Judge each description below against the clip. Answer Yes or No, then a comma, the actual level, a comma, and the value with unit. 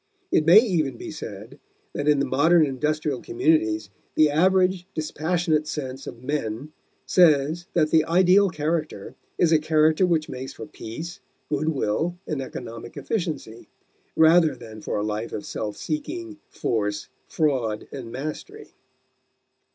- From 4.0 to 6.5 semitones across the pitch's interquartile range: Yes, average, 4.9 semitones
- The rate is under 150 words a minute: Yes, average, 140 wpm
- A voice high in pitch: No, medium, 155 Hz